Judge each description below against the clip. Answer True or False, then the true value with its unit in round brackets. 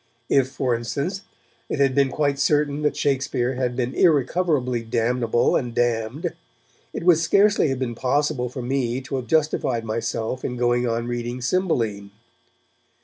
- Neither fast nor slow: True (150 wpm)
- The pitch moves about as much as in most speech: True (3.2 semitones)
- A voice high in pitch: False (130 Hz)